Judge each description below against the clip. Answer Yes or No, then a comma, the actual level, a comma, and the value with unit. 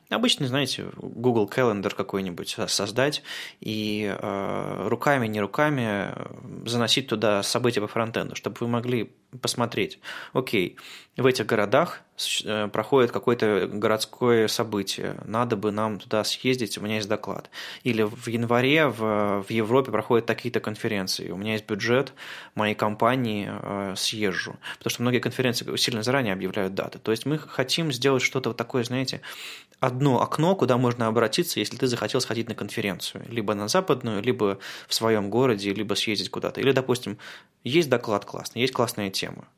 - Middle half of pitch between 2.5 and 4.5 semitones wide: Yes, average, 3.1 semitones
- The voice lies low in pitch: Yes, low, 115 Hz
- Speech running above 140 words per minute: Yes, average, 150 wpm